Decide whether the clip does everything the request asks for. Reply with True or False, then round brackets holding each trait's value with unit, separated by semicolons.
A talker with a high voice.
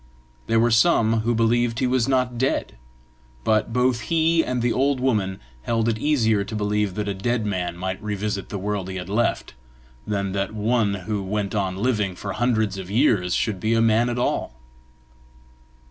False (110 Hz)